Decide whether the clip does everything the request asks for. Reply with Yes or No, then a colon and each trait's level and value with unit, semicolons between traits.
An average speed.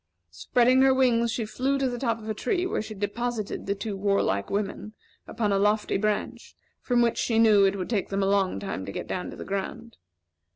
No: fast, 220 wpm